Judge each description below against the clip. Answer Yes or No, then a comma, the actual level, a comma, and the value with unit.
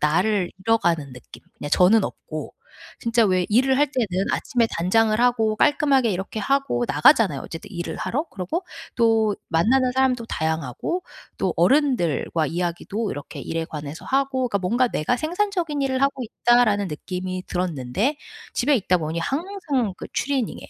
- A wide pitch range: Yes, wide, 7.0 semitones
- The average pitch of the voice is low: No, high, 220 Hz